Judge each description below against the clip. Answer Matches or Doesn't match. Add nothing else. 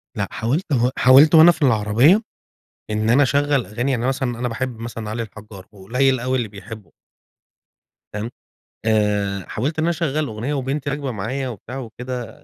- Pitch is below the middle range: Matches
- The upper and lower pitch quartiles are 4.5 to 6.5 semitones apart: Doesn't match